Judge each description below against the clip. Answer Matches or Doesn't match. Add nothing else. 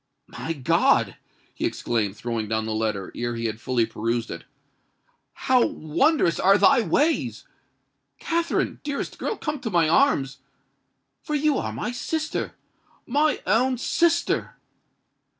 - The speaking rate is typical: Doesn't match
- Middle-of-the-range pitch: Matches